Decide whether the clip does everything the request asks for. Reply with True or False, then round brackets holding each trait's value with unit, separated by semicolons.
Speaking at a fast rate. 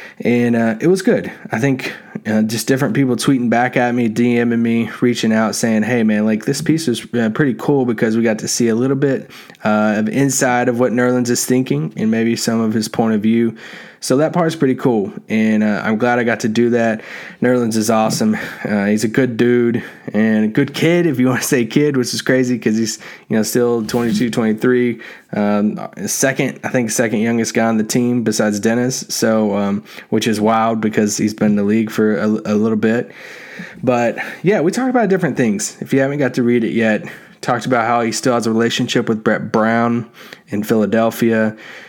True (215 wpm)